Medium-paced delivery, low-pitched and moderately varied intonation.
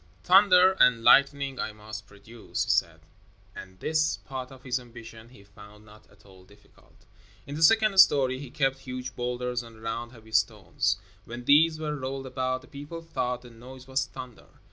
Yes: average, 180 wpm; low, 125 Hz; average, 3.8 semitones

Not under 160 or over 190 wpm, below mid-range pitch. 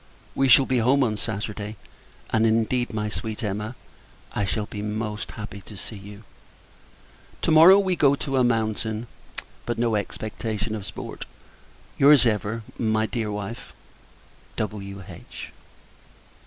No: average, 140 wpm; low, 110 Hz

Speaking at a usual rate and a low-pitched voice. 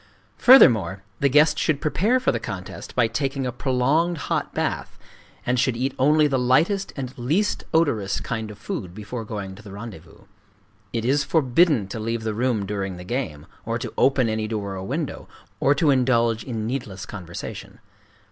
Yes: average, 175 wpm; low, 120 Hz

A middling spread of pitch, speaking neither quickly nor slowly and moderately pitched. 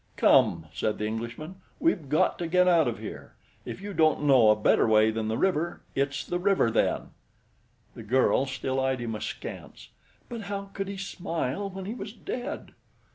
No: wide, 8.7 semitones; average, 185 wpm; medium, 155 Hz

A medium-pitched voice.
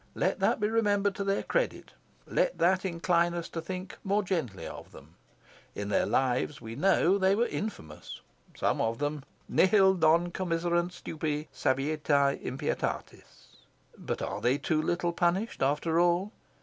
Yes: medium, 170 Hz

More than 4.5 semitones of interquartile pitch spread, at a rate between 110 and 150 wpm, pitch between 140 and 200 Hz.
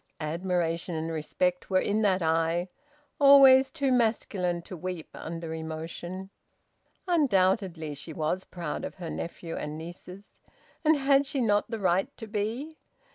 Yes: average, 5.3 semitones; average, 140 wpm; medium, 185 Hz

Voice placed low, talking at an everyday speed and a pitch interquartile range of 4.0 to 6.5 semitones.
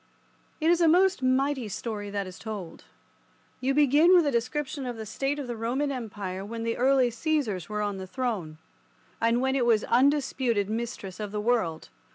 No: high, 235 Hz; average, 190 wpm; average, 4.6 semitones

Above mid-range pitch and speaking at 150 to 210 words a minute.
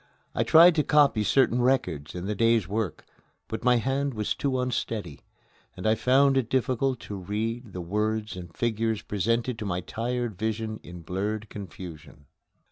No: low, 110 Hz; average, 165 wpm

